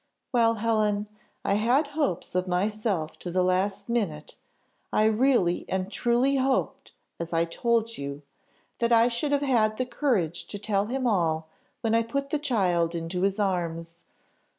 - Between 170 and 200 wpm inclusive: No, average, 155 wpm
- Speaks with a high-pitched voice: Yes, high, 210 Hz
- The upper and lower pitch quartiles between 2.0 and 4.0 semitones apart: No, average, 5.0 semitones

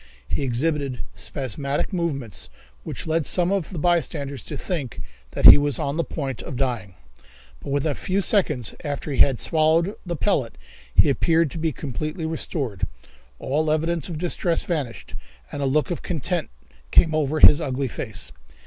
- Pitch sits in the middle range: Yes, medium, 150 Hz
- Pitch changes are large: No, average, 3.5 semitones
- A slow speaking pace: No, average, 165 wpm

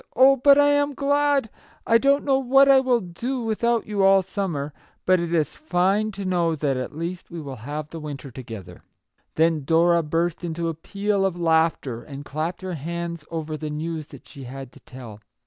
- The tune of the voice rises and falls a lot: Yes, wide, 6.1 semitones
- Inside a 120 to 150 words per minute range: No, average, 200 wpm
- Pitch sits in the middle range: Yes, medium, 170 Hz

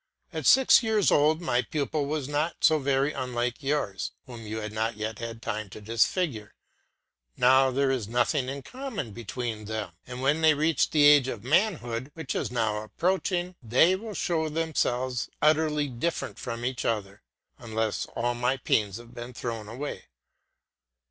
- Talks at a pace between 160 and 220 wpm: Yes, average, 165 wpm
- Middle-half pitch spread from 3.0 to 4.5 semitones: No, average, 5.0 semitones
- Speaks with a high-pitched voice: No, low, 130 Hz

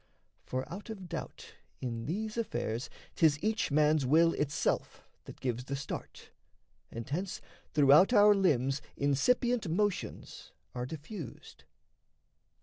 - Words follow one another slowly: Yes, slow, 120 wpm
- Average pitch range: No, wide, 6.9 semitones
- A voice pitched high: No, medium, 155 Hz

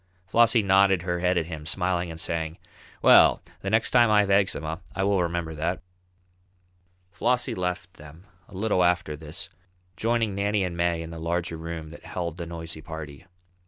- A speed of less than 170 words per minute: No, average, 175 wpm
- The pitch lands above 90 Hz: No, very low, 85 Hz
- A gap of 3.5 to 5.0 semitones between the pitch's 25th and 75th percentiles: No, average, 3.0 semitones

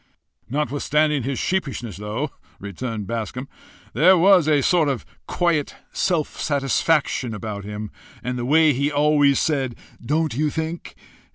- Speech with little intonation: No, average, 4.4 semitones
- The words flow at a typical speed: No, slow, 130 wpm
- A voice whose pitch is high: No, medium, 140 Hz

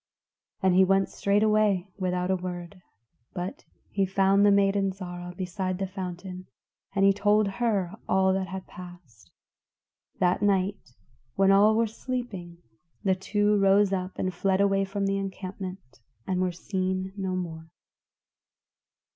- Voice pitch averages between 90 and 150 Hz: No, high, 190 Hz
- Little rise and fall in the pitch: Yes, narrow, 1.5 semitones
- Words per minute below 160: Yes, average, 140 wpm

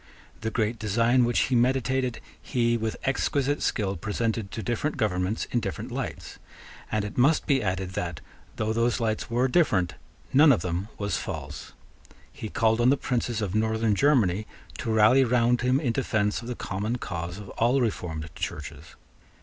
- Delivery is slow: No, average, 170 wpm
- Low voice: Yes, low, 115 Hz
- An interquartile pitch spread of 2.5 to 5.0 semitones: Yes, average, 3.2 semitones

